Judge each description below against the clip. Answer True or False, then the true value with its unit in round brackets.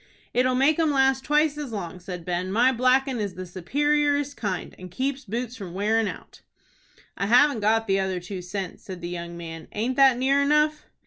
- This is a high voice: True (225 Hz)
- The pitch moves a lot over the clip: True (6.7 semitones)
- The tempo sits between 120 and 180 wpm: False (195 wpm)